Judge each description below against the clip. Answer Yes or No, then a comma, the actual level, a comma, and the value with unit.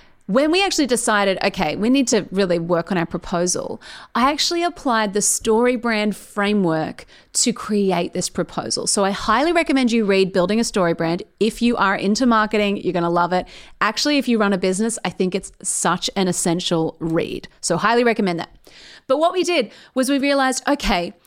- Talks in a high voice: Yes, high, 205 Hz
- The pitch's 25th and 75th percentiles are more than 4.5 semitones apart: Yes, average, 5.2 semitones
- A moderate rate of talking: Yes, average, 190 wpm